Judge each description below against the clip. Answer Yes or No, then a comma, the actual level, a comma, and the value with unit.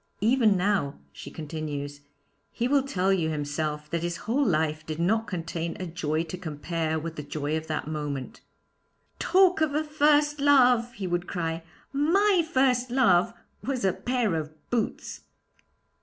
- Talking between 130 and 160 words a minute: Yes, average, 155 wpm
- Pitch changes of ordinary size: No, wide, 8.3 semitones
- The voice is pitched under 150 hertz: No, medium, 180 Hz